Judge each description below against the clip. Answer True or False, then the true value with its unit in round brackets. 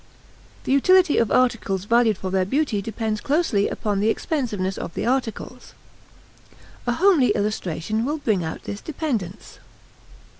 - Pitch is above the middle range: True (225 Hz)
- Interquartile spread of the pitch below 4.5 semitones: False (5.3 semitones)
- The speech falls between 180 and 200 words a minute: False (140 wpm)